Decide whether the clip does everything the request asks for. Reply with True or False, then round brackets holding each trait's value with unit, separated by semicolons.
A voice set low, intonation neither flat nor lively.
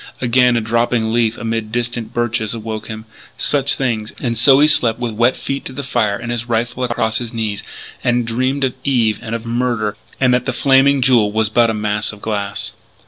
False (115 Hz; 2.1 semitones)